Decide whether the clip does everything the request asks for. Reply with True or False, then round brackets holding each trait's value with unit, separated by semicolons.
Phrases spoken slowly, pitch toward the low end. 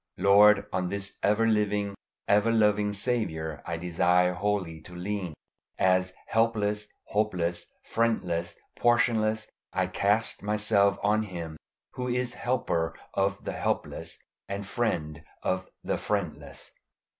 True (120 wpm; 100 Hz)